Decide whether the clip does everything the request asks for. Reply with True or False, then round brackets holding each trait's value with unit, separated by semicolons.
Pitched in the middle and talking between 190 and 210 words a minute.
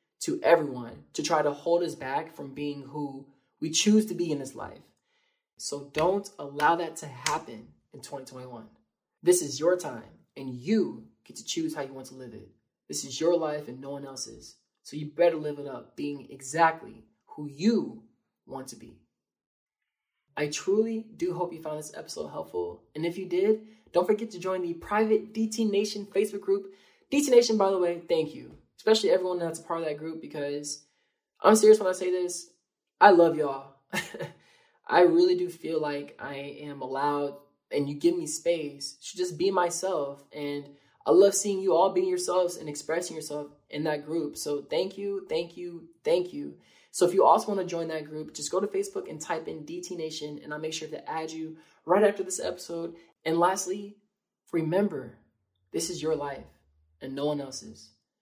True (165 Hz; 195 wpm)